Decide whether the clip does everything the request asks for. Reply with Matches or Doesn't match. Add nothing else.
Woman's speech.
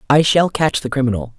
Matches